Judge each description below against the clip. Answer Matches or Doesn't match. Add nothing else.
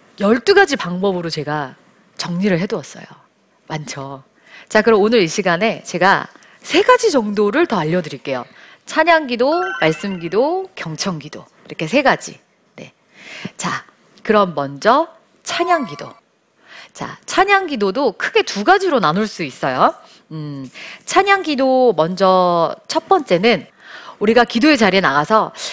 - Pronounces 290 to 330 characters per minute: Doesn't match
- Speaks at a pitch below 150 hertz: Doesn't match